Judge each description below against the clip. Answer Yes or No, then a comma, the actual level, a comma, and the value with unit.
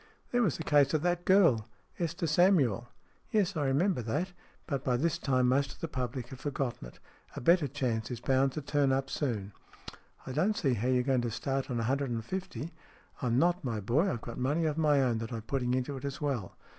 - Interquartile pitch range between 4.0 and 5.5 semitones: Yes, average, 4.6 semitones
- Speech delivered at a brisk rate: Yes, fast, 240 wpm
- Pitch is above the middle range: No, low, 135 Hz